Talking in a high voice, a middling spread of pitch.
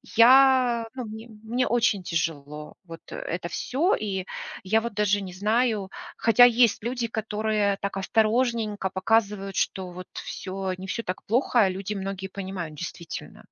Yes: high, 210 Hz; average, 3.5 semitones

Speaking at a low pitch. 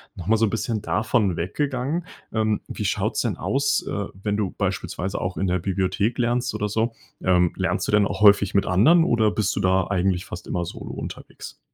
Yes: low, 105 Hz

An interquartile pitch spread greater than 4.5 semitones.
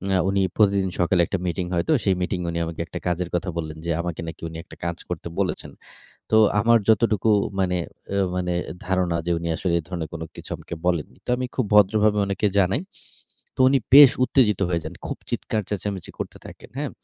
No: average, 3.4 semitones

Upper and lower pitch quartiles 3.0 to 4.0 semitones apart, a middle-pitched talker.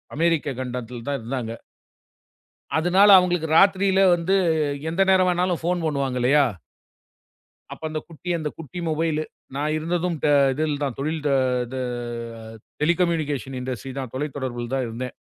No: average, 4.8 semitones; medium, 155 Hz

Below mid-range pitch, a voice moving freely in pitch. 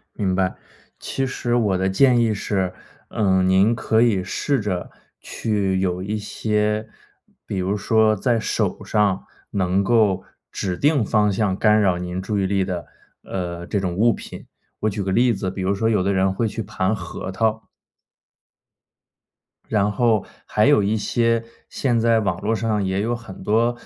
No: low, 105 Hz; average, 2.9 semitones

